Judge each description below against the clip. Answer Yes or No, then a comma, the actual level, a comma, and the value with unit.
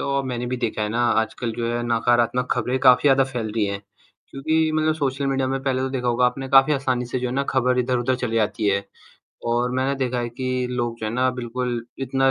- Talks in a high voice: No, low, 125 Hz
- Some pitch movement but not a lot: No, narrow, 1.9 semitones